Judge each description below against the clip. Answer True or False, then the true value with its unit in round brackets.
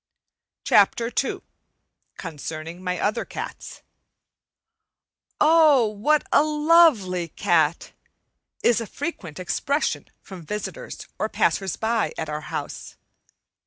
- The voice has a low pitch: False (210 Hz)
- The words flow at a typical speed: False (100 wpm)